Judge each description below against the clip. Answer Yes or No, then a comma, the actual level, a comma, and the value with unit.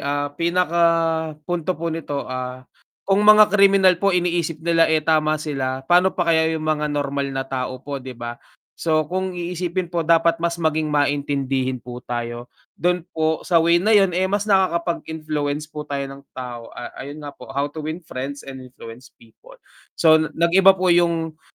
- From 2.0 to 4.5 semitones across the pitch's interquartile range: Yes, average, 3.7 semitones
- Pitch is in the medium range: Yes, medium, 155 Hz